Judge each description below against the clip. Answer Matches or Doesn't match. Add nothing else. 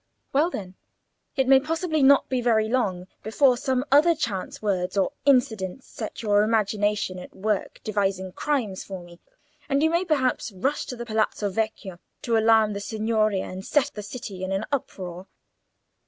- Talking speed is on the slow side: Doesn't match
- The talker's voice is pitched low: Doesn't match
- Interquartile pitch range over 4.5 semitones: Matches